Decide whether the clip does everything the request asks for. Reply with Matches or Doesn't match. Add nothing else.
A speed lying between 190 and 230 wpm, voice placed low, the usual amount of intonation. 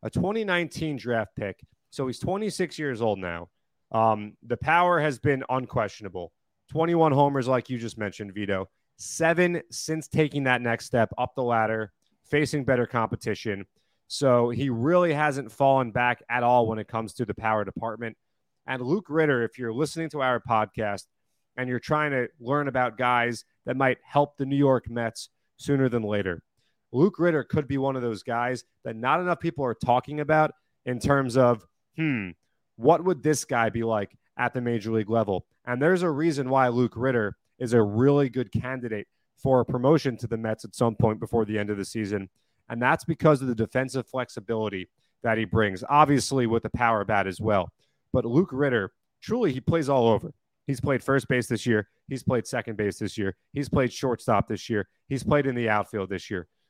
Matches